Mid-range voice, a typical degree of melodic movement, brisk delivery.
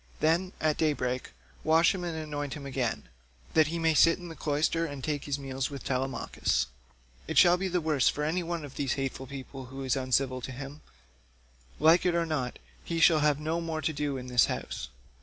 Yes: medium, 150 Hz; average, 3.4 semitones; fast, 215 wpm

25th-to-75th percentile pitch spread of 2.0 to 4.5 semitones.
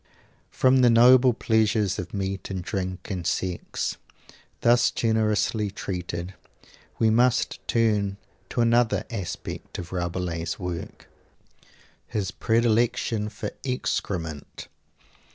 Yes: average, 4.1 semitones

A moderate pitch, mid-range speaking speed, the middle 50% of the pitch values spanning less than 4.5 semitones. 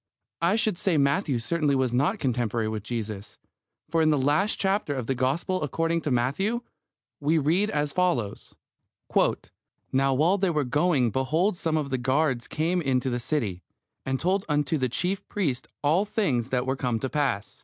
No: medium, 145 Hz; average, 180 wpm; average, 5.1 semitones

